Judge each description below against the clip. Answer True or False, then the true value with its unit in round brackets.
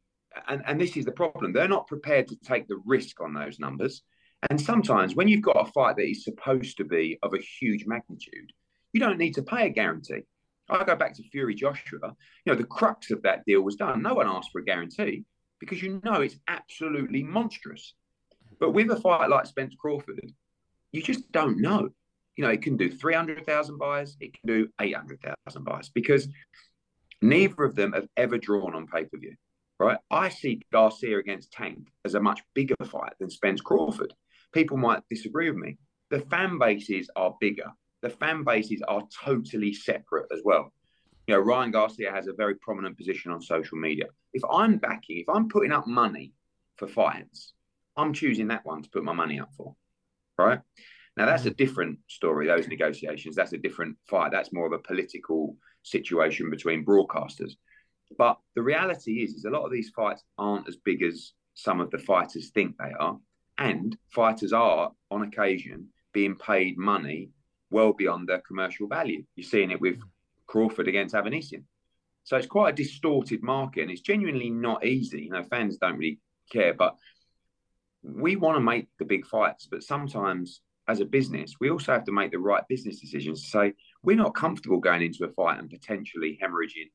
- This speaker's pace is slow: False (195 wpm)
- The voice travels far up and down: True (7.9 semitones)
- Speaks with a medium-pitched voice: False (115 Hz)